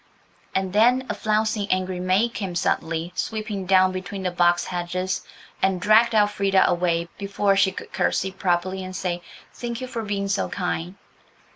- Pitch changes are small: Yes, narrow, 2.3 semitones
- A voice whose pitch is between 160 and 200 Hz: Yes, high, 190 Hz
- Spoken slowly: No, average, 160 wpm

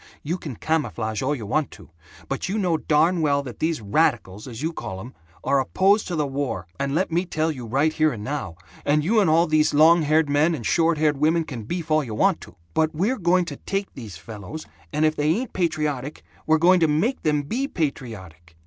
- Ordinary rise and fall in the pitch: Yes, average, 3.9 semitones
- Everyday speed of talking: No, fast, 225 wpm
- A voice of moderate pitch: Yes, medium, 155 Hz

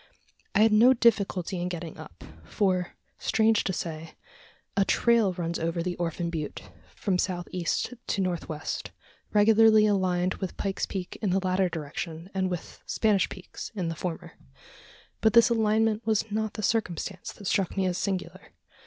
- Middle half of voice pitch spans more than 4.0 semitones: No, average, 3.4 semitones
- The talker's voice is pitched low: No, medium, 185 Hz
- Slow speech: No, average, 165 wpm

